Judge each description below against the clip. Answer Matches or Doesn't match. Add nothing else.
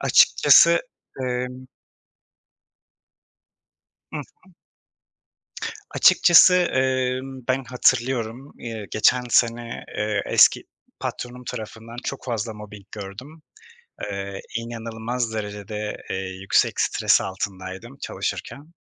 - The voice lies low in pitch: Matches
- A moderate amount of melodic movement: Matches